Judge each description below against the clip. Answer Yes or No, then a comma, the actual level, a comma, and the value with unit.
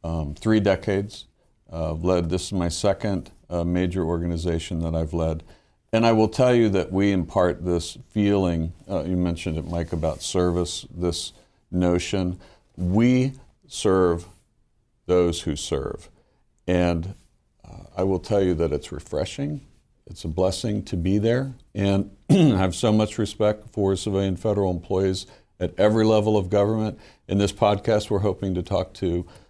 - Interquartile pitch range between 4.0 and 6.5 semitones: No, average, 3.3 semitones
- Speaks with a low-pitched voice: Yes, very low, 95 Hz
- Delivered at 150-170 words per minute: Yes, average, 160 wpm